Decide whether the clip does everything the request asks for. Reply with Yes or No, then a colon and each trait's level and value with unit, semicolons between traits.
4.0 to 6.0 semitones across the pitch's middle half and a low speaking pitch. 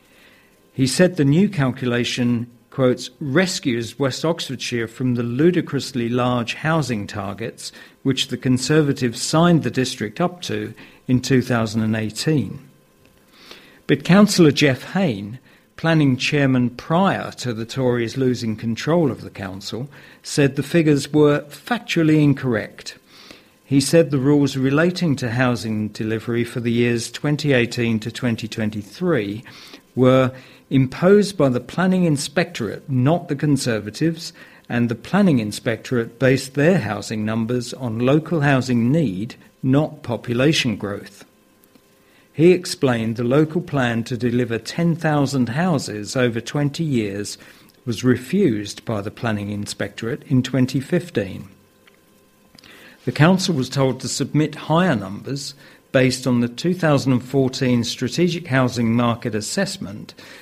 Yes: average, 4.3 semitones; low, 130 Hz